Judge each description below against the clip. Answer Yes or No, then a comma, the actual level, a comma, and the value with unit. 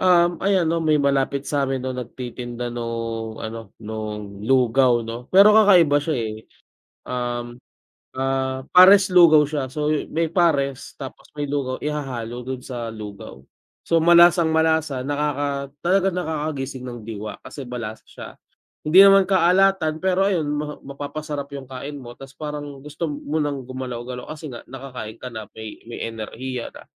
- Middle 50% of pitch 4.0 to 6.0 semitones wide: Yes, average, 4.5 semitones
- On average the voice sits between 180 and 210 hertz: No, medium, 140 Hz